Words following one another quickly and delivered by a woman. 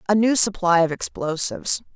No: average, 155 wpm; female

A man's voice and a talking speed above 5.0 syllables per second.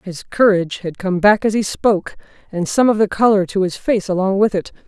No: female; 5.6 syllables/s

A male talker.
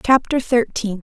No: female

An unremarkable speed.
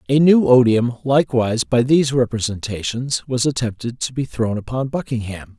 Yes: average, 150 wpm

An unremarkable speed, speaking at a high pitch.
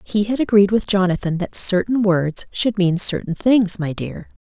Yes: average, 190 wpm; high, 195 Hz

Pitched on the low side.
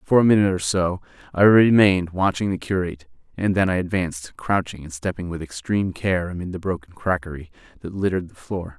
Yes: very low, 90 Hz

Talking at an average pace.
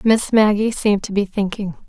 Yes: average, 190 wpm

